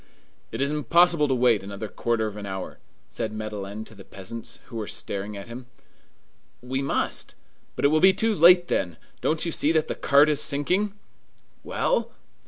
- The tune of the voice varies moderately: No, wide, 6.8 semitones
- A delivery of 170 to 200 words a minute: Yes, average, 185 wpm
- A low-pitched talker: Yes, low, 130 Hz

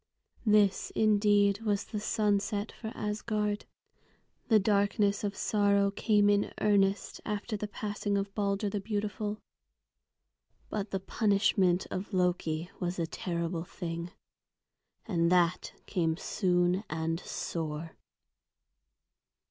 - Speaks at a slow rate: Yes, slow, 110 wpm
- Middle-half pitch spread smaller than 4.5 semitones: Yes, narrow, 2.6 semitones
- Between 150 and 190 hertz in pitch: No, high, 200 Hz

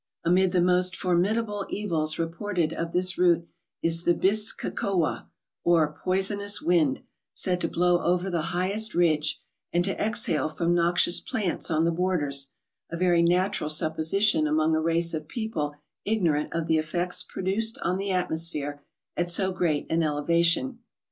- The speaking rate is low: No, average, 155 wpm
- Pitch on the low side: No, medium, 175 Hz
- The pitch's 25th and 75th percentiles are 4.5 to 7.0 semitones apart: No, average, 2.8 semitones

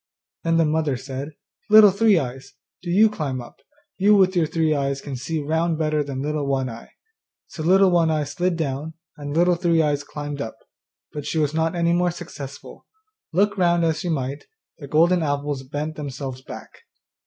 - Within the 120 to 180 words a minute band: No, average, 190 wpm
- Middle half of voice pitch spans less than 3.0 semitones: No, average, 3.4 semitones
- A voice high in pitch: No, medium, 155 Hz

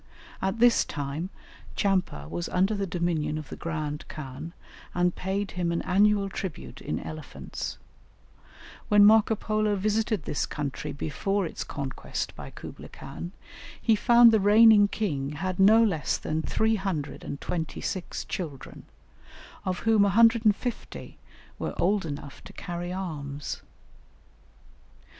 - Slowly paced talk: Yes, slow, 125 wpm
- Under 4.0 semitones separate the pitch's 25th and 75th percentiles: No, average, 5.3 semitones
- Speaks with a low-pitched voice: No, medium, 185 Hz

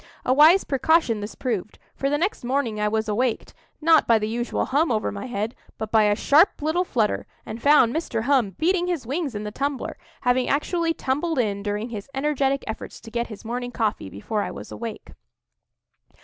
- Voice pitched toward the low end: No, high, 245 Hz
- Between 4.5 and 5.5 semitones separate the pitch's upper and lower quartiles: Yes, average, 5.1 semitones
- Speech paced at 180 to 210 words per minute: Yes, average, 190 wpm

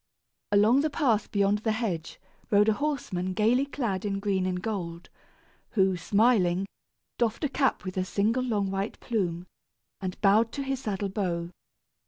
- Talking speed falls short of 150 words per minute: No, average, 160 wpm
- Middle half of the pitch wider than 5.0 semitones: No, average, 3.7 semitones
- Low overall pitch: No, high, 205 Hz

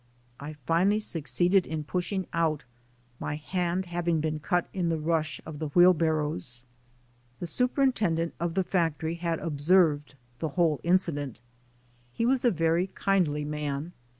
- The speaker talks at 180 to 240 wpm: No, average, 140 wpm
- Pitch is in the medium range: Yes, medium, 165 Hz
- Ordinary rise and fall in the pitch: Yes, average, 3.0 semitones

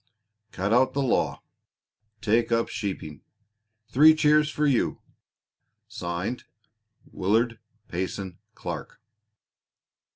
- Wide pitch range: Yes, wide, 6.3 semitones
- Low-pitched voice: Yes, low, 115 Hz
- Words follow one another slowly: Yes, slow, 95 wpm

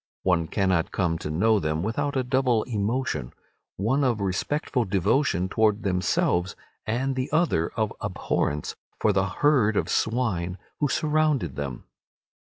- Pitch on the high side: No, low, 105 Hz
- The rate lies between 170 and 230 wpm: No, average, 140 wpm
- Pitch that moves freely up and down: Yes, wide, 6.3 semitones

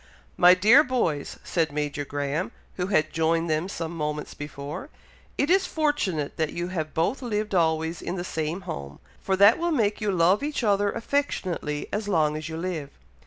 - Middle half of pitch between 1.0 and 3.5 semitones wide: No, average, 5.1 semitones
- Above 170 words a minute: Yes, average, 180 wpm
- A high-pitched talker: No, medium, 175 Hz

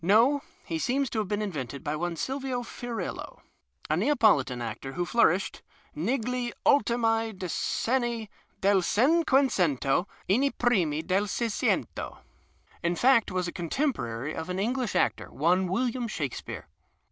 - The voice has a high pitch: Yes, high, 210 Hz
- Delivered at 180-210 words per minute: No, average, 145 wpm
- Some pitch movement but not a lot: No, wide, 6.2 semitones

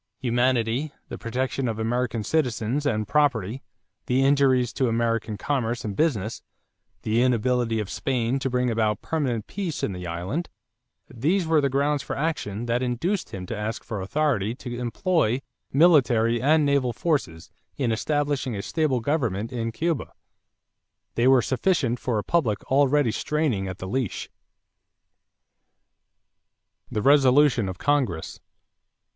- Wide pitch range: No, average, 4.3 semitones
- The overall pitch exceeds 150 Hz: No, low, 125 Hz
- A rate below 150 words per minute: Yes, average, 140 wpm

